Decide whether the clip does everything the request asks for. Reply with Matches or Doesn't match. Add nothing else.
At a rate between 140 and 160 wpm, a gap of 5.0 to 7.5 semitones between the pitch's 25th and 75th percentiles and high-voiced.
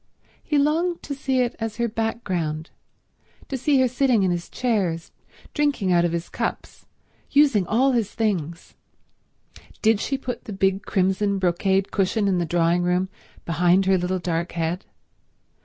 Matches